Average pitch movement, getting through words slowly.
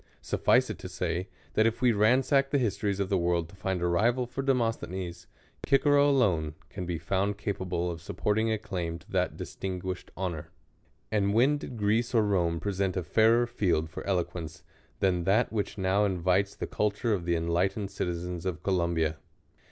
No: average, 4.0 semitones; average, 180 wpm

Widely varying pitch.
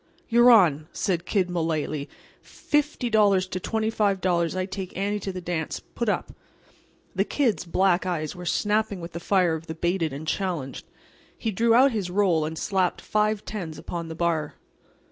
No: average, 4.0 semitones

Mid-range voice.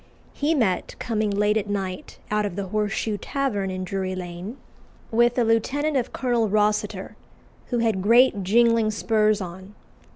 No: high, 210 Hz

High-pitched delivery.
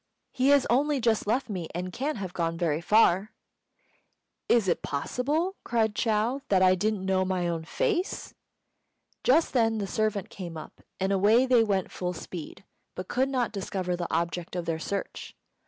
Yes: high, 200 Hz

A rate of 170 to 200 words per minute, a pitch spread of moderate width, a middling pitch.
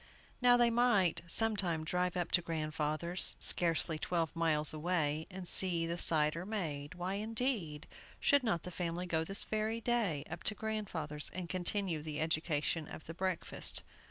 No: average, 160 wpm; average, 4.1 semitones; medium, 175 Hz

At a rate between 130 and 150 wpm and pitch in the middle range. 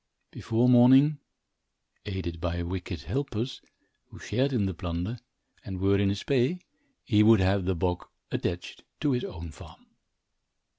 No: average, 145 wpm; low, 100 Hz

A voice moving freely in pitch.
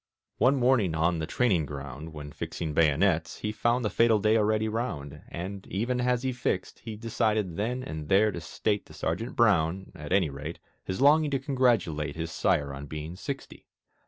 Yes: wide, 7.0 semitones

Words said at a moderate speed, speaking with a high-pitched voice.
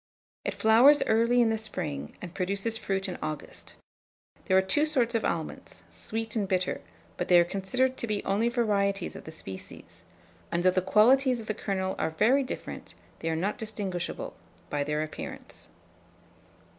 Yes: average, 170 wpm; high, 200 Hz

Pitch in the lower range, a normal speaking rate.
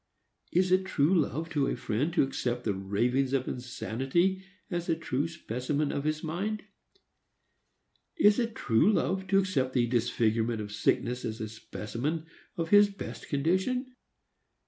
No: medium, 145 Hz; average, 150 wpm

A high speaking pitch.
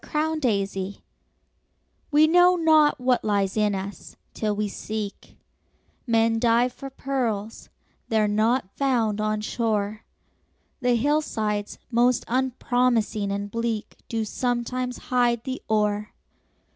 Yes: high, 230 Hz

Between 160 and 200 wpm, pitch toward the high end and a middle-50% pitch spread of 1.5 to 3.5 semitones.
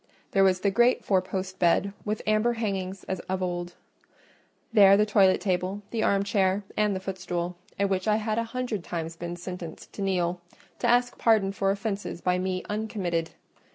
Yes: average, 180 wpm; high, 195 Hz; narrow, 2.5 semitones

